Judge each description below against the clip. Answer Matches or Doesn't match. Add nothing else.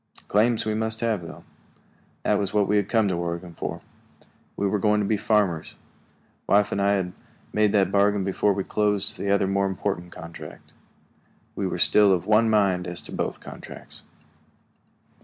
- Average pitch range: Doesn't match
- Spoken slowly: Doesn't match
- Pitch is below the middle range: Matches